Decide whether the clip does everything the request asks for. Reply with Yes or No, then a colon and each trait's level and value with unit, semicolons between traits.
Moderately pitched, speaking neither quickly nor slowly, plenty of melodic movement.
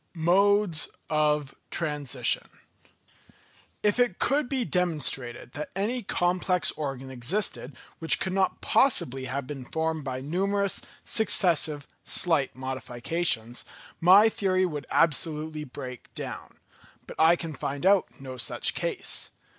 No: medium, 160 Hz; slow, 120 wpm; wide, 5.7 semitones